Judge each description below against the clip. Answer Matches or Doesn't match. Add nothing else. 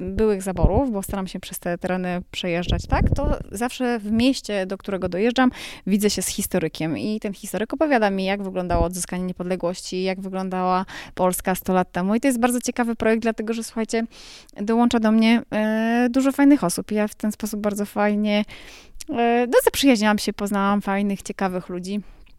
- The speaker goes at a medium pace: Doesn't match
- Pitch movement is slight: Doesn't match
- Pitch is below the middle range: Doesn't match